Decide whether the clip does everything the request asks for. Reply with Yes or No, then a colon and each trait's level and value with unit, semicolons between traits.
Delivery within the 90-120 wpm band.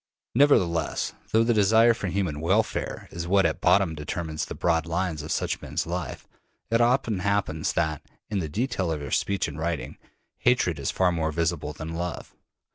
No: average, 180 wpm